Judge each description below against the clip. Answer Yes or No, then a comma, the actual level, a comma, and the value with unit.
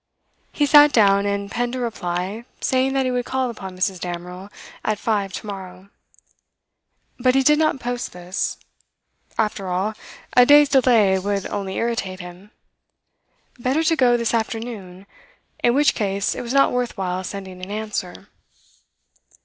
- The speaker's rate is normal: Yes, average, 155 wpm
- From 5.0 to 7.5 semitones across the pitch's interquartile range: No, average, 4.6 semitones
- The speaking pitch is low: No, high, 210 Hz